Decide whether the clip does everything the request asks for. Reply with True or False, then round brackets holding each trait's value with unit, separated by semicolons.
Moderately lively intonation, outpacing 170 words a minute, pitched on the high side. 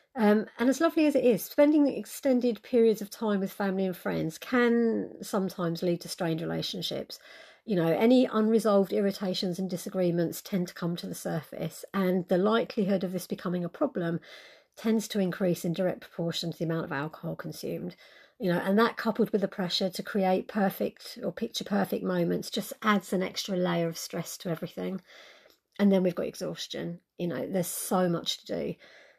True (4.0 semitones; 190 wpm; 195 Hz)